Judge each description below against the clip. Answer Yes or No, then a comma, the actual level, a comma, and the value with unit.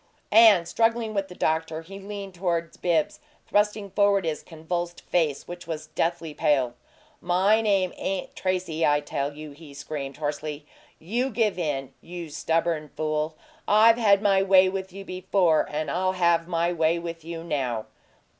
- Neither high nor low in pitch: Yes, medium, 170 Hz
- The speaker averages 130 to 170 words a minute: Yes, average, 160 wpm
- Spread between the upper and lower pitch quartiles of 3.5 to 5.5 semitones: Yes, average, 3.8 semitones